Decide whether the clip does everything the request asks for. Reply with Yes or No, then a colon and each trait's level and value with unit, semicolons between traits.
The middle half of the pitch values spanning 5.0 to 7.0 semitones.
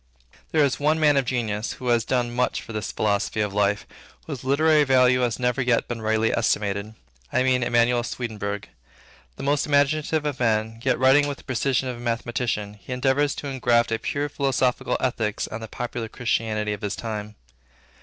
No: average, 3.3 semitones